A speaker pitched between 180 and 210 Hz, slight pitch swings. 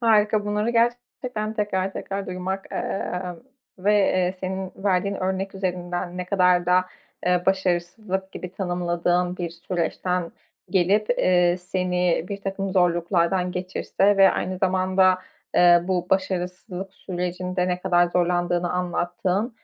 Yes: medium, 185 Hz; narrow, 1.5 semitones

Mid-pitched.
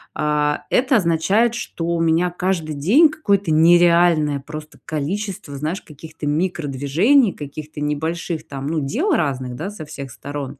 Yes: medium, 160 Hz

